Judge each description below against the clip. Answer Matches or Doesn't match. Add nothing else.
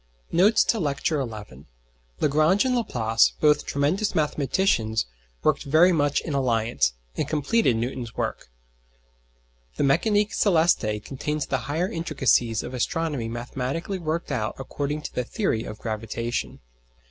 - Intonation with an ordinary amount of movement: Doesn't match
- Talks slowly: Matches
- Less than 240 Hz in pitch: Matches